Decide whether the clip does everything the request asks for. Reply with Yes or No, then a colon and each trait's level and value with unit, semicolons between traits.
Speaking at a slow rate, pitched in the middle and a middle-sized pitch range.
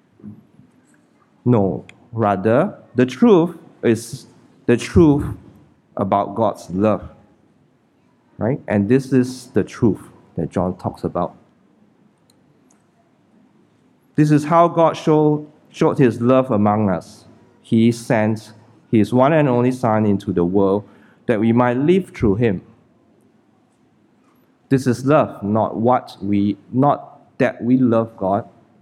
No: slow, 120 wpm; low, 120 Hz; average, 4.4 semitones